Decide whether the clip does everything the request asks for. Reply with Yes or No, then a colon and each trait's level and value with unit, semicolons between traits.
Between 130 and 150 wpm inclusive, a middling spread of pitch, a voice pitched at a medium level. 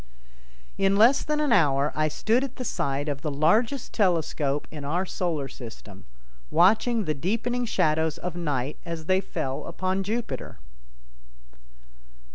No: average, 140 wpm; wide, 6.9 semitones; medium, 170 Hz